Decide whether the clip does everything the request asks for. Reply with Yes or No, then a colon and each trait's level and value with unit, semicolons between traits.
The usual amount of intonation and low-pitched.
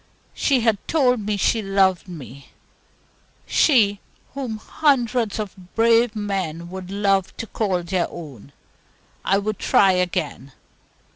No: average, 3.8 semitones; high, 200 Hz